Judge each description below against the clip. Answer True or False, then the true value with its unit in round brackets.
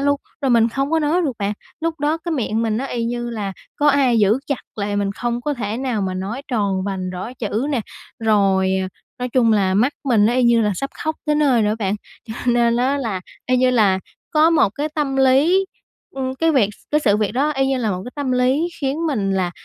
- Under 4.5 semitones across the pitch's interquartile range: False (5.0 semitones)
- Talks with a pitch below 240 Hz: False (245 Hz)